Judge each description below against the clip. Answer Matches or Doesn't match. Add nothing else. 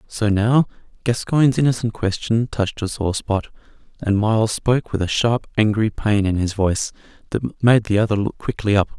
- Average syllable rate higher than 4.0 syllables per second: Matches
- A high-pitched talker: Doesn't match